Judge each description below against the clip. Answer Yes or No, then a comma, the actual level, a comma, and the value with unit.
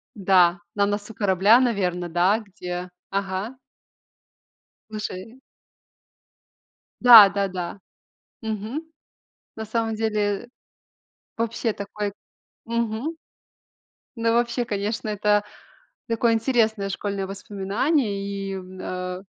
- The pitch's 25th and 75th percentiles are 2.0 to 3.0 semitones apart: Yes, narrow, 2.6 semitones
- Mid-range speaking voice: No, high, 205 Hz